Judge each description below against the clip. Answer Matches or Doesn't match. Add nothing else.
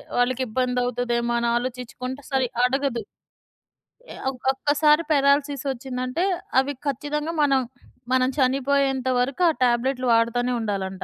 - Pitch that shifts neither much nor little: Doesn't match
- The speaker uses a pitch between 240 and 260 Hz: Matches